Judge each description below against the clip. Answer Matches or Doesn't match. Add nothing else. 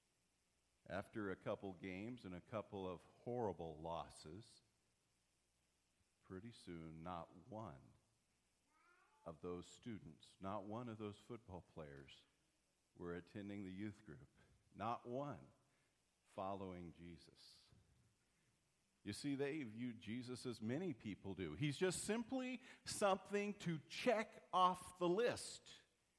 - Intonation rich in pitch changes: Matches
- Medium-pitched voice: Doesn't match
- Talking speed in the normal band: Doesn't match